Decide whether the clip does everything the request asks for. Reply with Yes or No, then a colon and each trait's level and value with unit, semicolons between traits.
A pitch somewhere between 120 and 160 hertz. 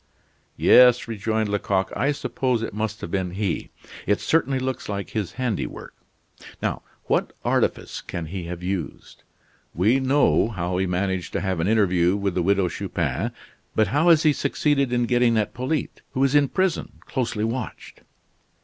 No: low, 110 Hz